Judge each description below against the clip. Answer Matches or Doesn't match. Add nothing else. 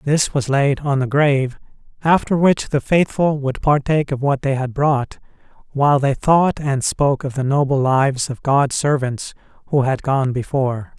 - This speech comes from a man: Matches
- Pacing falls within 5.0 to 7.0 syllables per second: Doesn't match